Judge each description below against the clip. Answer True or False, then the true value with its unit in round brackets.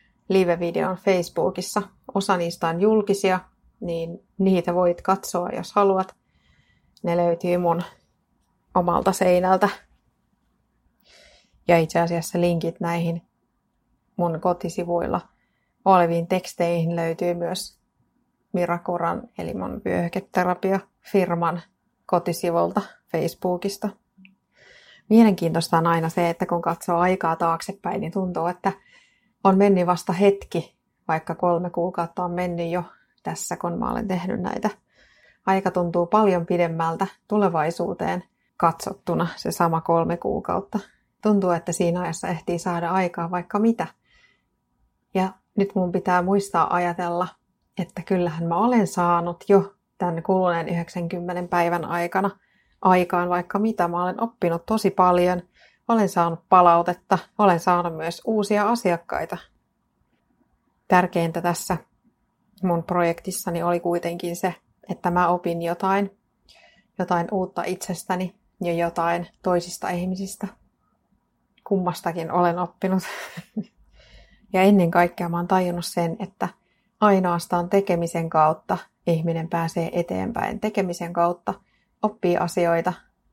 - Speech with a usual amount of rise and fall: False (1.9 semitones)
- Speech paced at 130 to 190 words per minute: False (110 wpm)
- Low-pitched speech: False (180 Hz)